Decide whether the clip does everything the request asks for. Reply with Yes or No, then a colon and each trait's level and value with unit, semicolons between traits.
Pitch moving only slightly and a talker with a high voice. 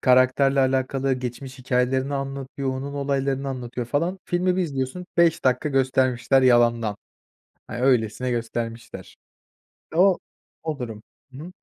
No: narrow, 1.9 semitones; low, 130 Hz